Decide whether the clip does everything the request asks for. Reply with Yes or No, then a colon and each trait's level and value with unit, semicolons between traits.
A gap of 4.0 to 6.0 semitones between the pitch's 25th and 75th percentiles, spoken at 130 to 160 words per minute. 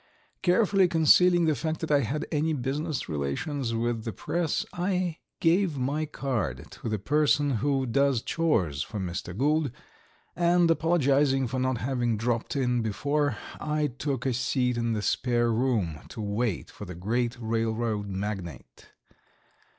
Yes: average, 5.3 semitones; average, 150 wpm